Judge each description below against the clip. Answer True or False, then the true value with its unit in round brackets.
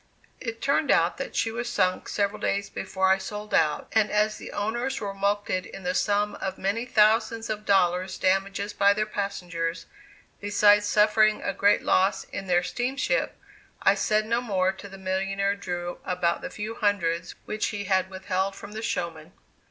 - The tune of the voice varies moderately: False (2.1 semitones)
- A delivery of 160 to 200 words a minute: True (175 wpm)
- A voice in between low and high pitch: False (200 Hz)